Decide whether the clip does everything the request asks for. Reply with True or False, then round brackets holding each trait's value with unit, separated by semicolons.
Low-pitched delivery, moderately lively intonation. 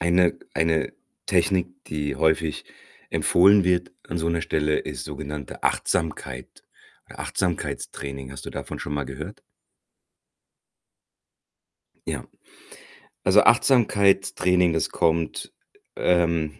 True (85 Hz; 3.3 semitones)